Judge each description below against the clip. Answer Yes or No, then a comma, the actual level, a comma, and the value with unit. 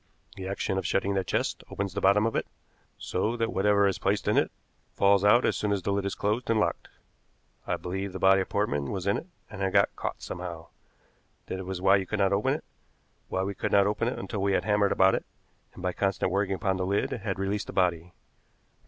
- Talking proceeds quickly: Yes, fast, 235 wpm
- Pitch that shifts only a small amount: Yes, narrow, 1.3 semitones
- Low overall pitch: Yes, low, 100 Hz